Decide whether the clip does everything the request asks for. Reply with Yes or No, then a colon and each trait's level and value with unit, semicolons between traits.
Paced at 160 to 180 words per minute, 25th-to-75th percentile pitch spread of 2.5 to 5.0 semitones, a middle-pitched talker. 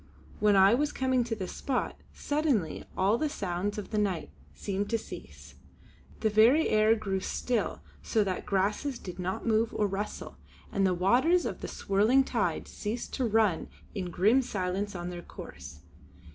No: average, 170 wpm; average, 3.9 semitones; high, 210 Hz